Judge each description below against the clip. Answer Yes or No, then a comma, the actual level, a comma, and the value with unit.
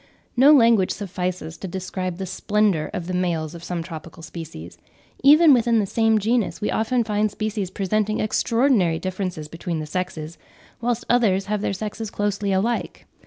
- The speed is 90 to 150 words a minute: No, average, 165 wpm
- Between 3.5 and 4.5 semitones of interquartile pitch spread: Yes, average, 3.9 semitones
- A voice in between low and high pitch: No, high, 195 Hz